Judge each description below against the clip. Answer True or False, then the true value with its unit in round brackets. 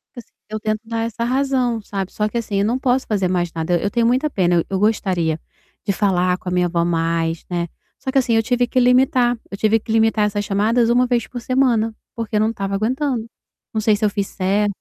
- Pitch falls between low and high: False (215 Hz)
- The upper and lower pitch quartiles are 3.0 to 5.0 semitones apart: True (3.9 semitones)